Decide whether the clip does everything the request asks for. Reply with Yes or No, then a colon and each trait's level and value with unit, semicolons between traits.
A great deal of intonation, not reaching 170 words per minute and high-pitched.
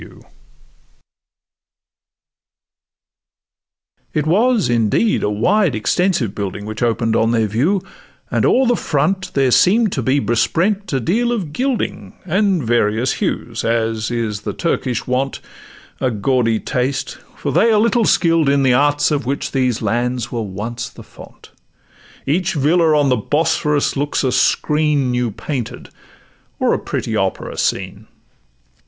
No: wide, 6.5 semitones; average, 140 wpm; low, 135 Hz